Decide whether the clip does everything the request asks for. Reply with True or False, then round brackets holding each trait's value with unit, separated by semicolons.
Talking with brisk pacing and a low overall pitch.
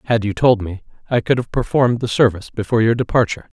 True (215 wpm; 115 Hz)